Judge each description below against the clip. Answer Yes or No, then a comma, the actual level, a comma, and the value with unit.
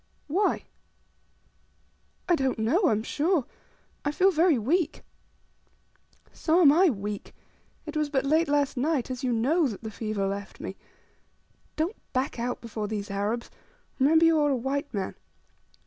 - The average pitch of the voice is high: Yes, very high, 275 Hz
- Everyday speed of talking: Yes, average, 155 wpm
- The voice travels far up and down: Yes, wide, 6.0 semitones